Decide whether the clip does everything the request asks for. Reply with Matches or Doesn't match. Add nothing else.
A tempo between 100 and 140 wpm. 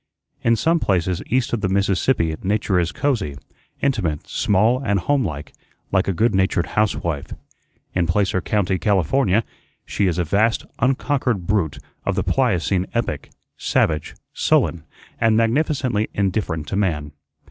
Matches